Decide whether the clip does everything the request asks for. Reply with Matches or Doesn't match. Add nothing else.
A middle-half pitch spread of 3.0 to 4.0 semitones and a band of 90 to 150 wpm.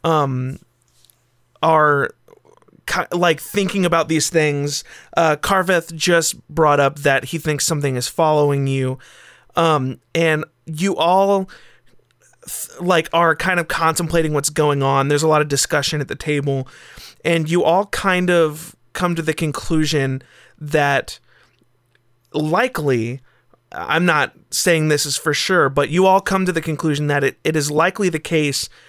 Matches